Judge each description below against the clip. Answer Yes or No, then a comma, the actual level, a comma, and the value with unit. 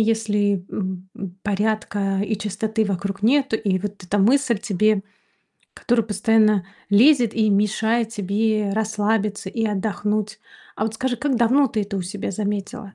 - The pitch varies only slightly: Yes, narrow, 1.9 semitones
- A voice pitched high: Yes, high, 210 Hz